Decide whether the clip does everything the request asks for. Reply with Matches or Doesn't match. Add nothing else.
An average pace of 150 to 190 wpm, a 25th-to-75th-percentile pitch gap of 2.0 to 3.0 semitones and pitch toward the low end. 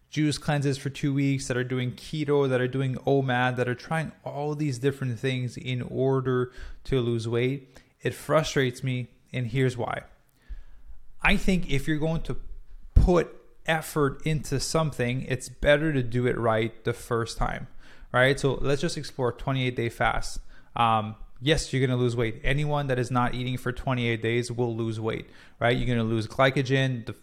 Matches